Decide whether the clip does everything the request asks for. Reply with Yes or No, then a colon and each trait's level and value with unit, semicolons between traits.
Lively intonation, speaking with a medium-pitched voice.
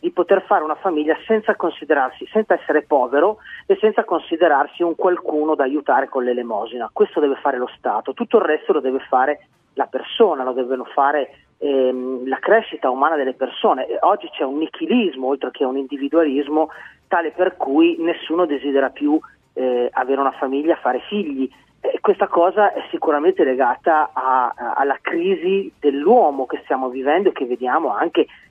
Yes: wide, 6.9 semitones; medium, 155 Hz